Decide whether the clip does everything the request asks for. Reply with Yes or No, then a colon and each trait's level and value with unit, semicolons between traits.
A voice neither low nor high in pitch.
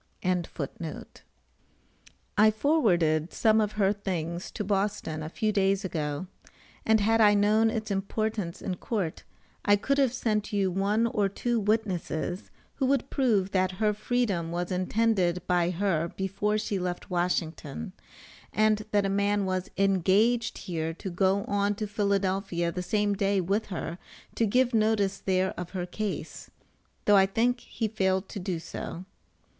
No: high, 200 Hz